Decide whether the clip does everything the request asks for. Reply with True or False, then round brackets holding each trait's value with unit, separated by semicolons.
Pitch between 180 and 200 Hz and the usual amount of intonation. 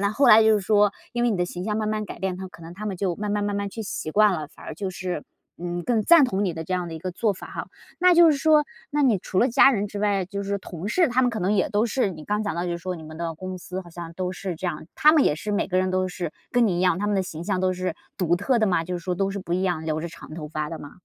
True (190 Hz; 3.4 semitones)